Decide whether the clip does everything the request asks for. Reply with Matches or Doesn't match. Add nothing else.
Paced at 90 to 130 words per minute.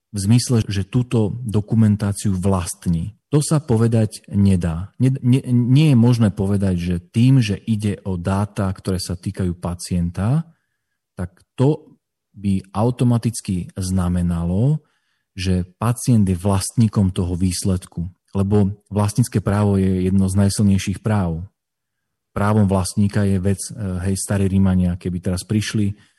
Matches